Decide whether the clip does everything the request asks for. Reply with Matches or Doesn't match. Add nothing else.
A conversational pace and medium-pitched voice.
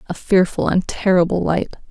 Matches